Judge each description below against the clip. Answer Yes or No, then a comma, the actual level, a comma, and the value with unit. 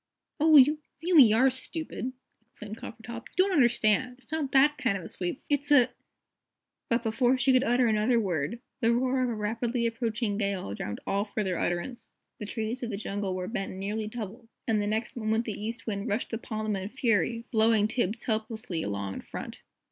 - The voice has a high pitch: Yes, high, 225 Hz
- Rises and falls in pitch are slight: No, average, 3.2 semitones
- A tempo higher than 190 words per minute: Yes, average, 200 wpm